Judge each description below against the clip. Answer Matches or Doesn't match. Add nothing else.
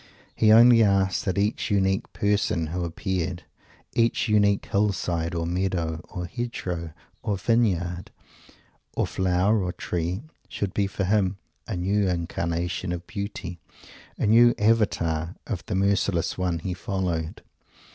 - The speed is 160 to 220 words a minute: Doesn't match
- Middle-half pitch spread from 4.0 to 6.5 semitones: Doesn't match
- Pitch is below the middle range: Matches